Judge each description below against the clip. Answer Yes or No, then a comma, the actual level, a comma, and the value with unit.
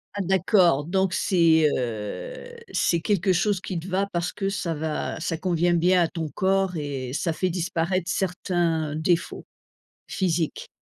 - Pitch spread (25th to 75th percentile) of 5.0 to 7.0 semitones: No, average, 2.7 semitones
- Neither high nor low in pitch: Yes, medium, 175 Hz